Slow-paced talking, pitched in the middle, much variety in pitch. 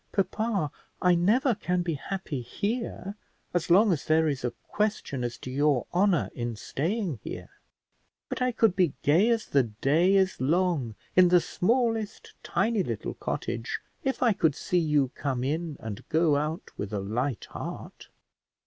No: average, 165 wpm; medium, 170 Hz; wide, 6.5 semitones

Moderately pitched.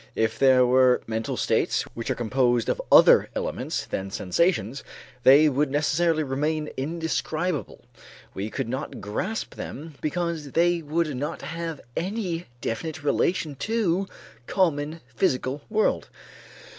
Yes: medium, 150 Hz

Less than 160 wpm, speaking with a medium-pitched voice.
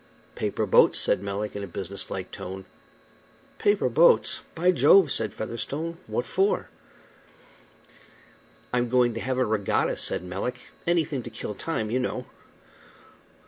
No: average, 140 wpm; low, 120 Hz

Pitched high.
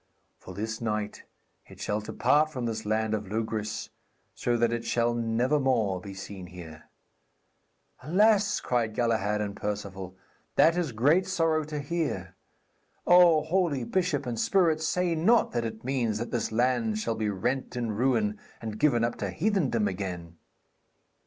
No: low, 115 Hz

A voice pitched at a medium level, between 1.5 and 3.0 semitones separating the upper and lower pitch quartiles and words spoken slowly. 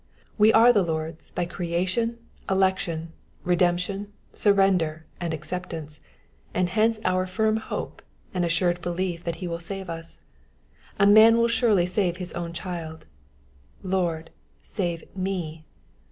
Yes: medium, 180 Hz; average, 2.7 semitones; slow, 130 wpm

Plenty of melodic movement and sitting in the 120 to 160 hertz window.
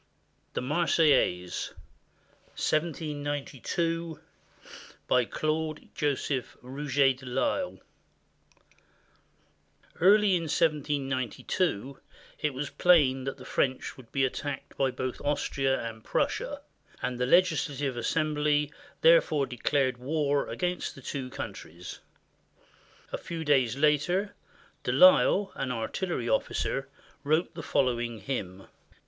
No: average, 3.6 semitones; medium, 140 Hz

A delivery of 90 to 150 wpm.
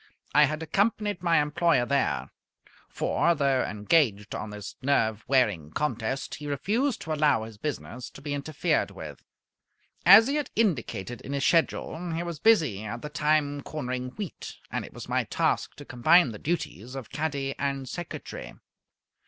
No: average, 160 wpm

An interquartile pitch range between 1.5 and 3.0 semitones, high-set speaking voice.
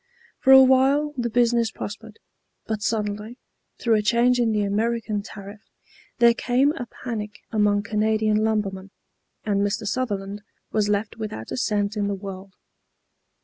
Yes: narrow, 2.5 semitones; high, 215 Hz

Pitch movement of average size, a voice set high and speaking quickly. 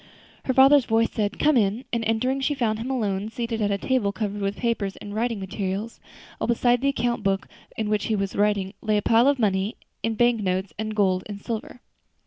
Yes: average, 3.0 semitones; high, 220 Hz; fast, 215 wpm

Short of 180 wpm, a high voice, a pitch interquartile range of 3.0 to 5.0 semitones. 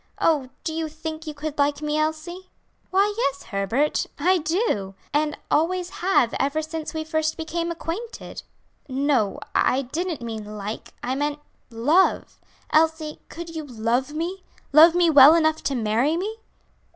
Yes: average, 150 wpm; very high, 310 Hz; average, 3.5 semitones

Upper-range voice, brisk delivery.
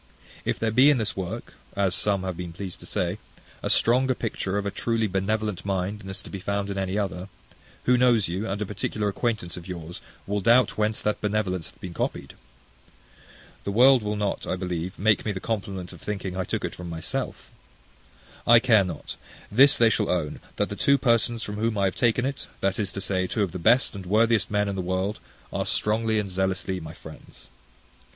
No: low, 100 Hz; fast, 215 wpm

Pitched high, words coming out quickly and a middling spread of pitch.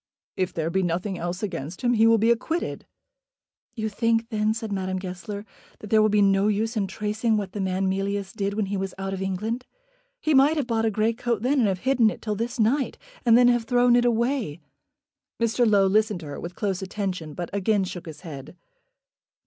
Yes: high, 210 Hz; fast, 215 wpm; average, 3.3 semitones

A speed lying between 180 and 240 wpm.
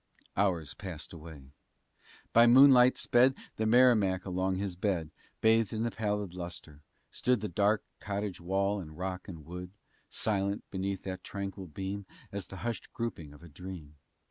No: average, 150 wpm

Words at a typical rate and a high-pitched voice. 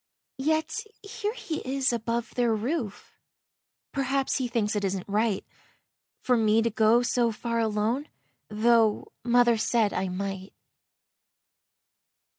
No: slow, 120 wpm; high, 230 Hz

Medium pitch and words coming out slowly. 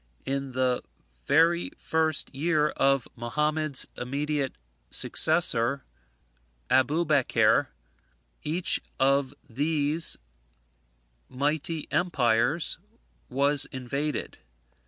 Yes: medium, 145 Hz; slow, 70 wpm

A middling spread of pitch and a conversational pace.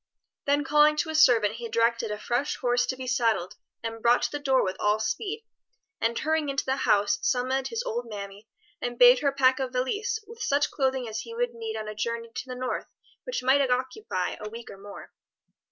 No: average, 4.2 semitones; fast, 215 wpm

